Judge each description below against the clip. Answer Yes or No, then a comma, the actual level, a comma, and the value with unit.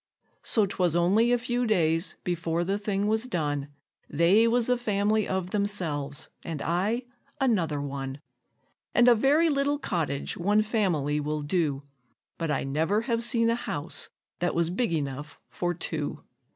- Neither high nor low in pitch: Yes, medium, 180 Hz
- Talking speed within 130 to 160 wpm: Yes, average, 155 wpm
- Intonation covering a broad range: Yes, wide, 6.5 semitones